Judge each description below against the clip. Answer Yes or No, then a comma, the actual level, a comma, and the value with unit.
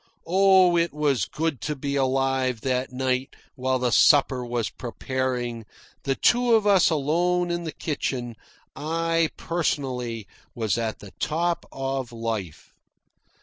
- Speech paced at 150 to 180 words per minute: No, slow, 135 wpm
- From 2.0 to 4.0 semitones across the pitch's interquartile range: No, average, 5.0 semitones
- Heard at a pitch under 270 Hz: Yes, low, 135 Hz